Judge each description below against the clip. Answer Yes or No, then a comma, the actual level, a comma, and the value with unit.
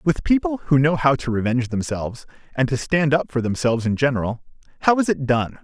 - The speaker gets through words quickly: Yes, fast, 215 wpm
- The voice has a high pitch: No, medium, 140 Hz